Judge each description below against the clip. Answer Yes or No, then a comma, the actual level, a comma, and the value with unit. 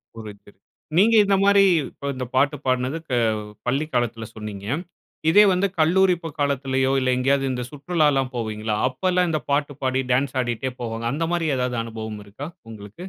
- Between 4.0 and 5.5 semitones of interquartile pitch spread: Yes, average, 4.7 semitones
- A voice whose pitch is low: Yes, low, 130 Hz